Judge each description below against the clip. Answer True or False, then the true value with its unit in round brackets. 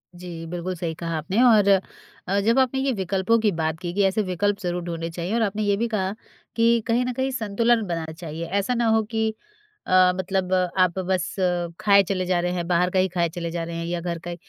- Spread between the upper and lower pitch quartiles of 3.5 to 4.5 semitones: True (4.0 semitones)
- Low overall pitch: False (185 Hz)